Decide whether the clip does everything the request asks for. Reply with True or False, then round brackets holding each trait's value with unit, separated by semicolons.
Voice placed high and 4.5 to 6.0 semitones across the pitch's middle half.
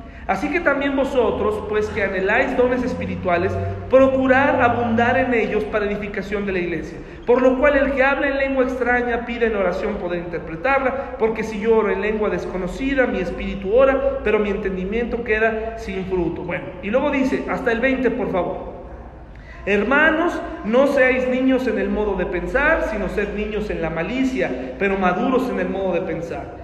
True (220 Hz; 5.3 semitones)